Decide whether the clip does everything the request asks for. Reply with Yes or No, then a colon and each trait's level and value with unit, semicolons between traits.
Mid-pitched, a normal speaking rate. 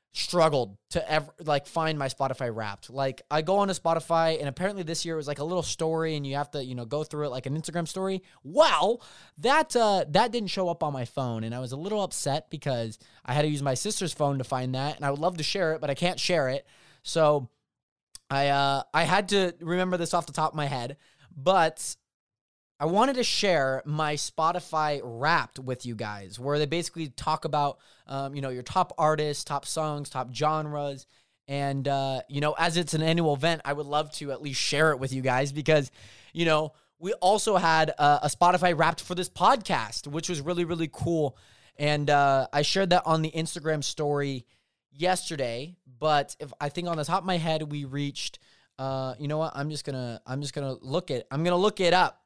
No: medium, 150 Hz; fast, 225 wpm